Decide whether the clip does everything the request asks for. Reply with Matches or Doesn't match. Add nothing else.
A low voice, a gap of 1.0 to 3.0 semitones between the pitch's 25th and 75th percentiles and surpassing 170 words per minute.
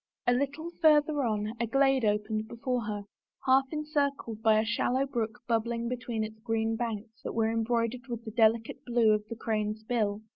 Doesn't match